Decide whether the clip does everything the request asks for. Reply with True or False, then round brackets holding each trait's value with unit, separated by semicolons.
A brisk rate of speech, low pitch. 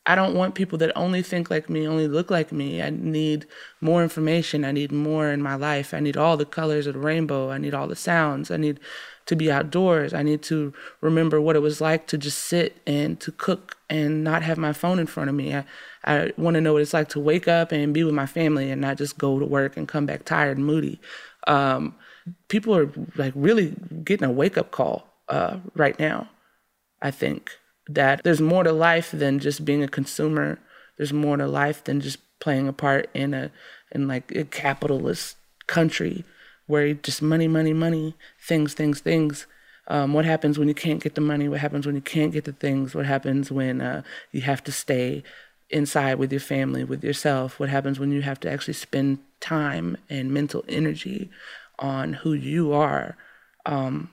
False (210 wpm; 150 Hz)